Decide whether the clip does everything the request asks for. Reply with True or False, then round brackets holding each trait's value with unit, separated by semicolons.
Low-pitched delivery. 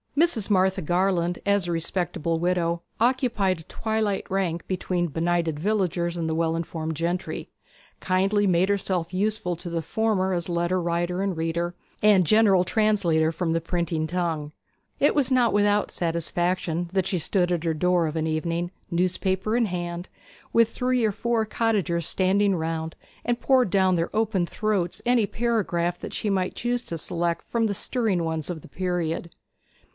False (180 Hz)